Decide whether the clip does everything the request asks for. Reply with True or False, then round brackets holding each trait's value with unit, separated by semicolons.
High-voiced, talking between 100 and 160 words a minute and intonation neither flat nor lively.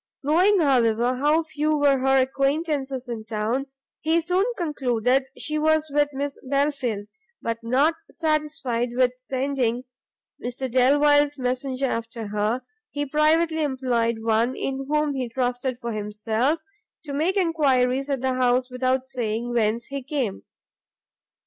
True (265 Hz; 135 wpm; 3.3 semitones)